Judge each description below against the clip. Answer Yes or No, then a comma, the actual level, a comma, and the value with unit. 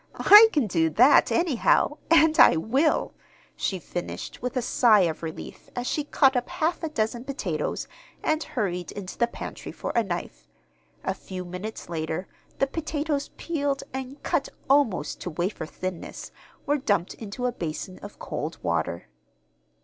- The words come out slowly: No, average, 155 wpm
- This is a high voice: Yes, high, 230 Hz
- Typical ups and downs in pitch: No, wide, 8.2 semitones